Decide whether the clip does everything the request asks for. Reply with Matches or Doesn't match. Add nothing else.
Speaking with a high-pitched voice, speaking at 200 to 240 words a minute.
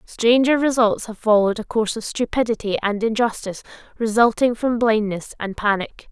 Doesn't match